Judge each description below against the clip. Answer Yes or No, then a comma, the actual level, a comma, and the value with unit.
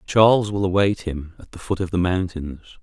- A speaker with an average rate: No, fast, 210 wpm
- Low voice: Yes, very low, 95 Hz